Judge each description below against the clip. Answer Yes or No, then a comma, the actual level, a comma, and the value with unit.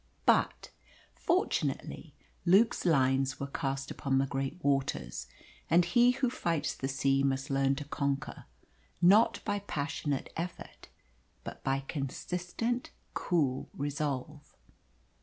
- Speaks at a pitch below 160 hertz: Yes, medium, 140 Hz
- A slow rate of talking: Yes, slow, 115 wpm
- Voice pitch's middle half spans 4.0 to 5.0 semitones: Yes, average, 4.5 semitones